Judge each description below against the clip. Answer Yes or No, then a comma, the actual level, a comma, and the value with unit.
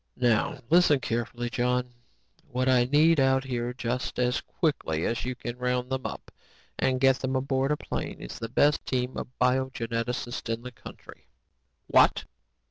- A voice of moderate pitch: No, low, 125 Hz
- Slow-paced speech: No, average, 160 wpm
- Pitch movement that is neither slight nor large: No, narrow, 1.5 semitones